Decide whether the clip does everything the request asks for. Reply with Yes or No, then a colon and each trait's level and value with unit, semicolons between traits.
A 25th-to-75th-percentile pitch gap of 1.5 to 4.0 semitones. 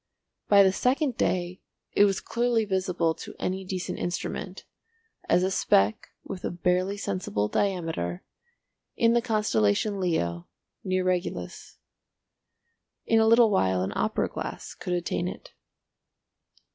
Yes: average, 2.9 semitones